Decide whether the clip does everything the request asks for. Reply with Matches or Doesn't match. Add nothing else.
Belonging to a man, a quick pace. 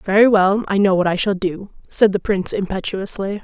Doesn't match